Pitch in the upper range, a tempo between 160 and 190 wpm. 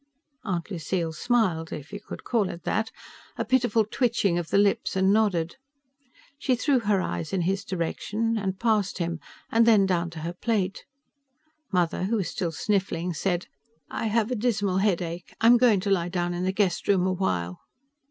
Yes: high, 195 Hz; average, 180 wpm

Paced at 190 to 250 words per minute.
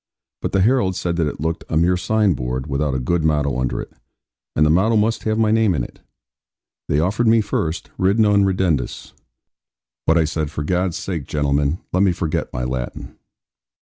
Yes: average, 195 wpm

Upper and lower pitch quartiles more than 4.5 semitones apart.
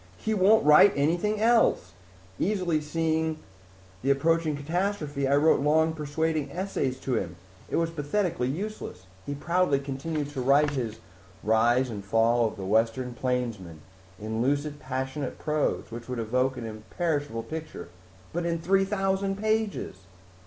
Yes: average, 5.2 semitones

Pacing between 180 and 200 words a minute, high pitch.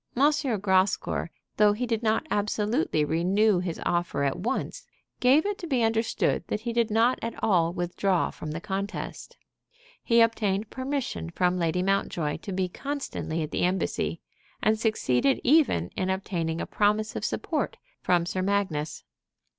No: average, 155 wpm; high, 200 Hz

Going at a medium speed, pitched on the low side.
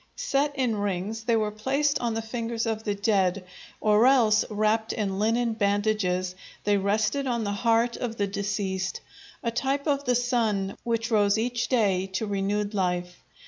No: average, 170 wpm; high, 215 Hz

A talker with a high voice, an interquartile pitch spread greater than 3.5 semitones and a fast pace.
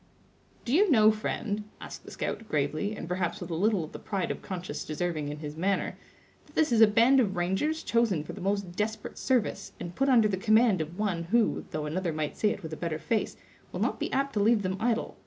Yes: high, 200 Hz; average, 4.6 semitones; fast, 235 wpm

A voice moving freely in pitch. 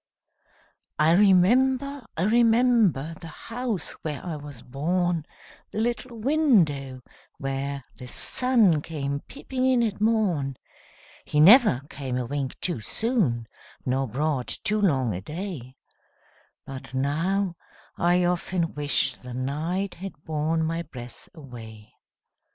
Yes: wide, 7.4 semitones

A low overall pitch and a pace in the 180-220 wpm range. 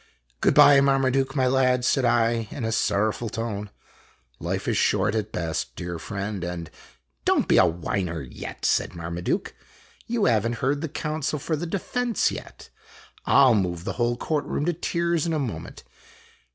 Yes: low, 120 Hz; average, 185 wpm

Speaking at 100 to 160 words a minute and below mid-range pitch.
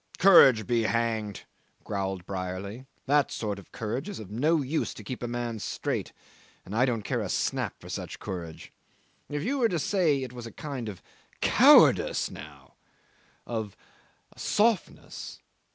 Yes: average, 155 wpm; low, 120 Hz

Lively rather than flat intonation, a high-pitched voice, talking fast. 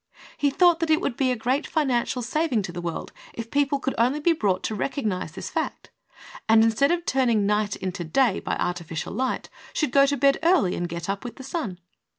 Yes: wide, 6.2 semitones; high, 245 Hz; fast, 215 wpm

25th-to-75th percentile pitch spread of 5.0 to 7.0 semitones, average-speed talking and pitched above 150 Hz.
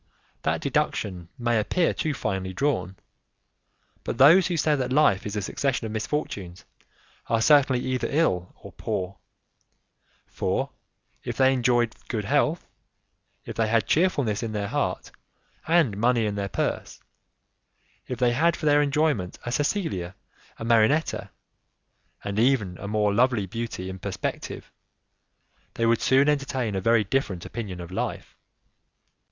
No: wide, 5.5 semitones; average, 145 wpm; low, 115 Hz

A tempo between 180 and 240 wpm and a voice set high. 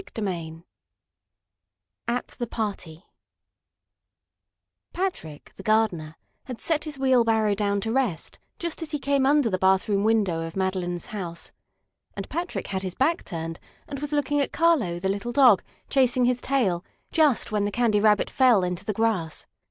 No: average, 160 wpm; high, 215 Hz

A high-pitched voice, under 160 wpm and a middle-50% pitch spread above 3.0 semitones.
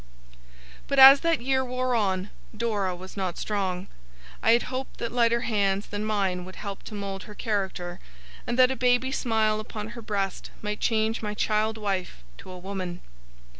No: high, 215 Hz; average, 175 wpm; average, 3.5 semitones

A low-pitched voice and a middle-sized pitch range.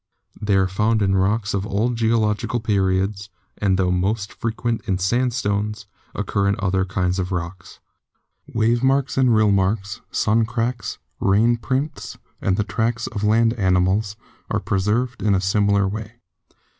Yes: low, 105 Hz; average, 3.0 semitones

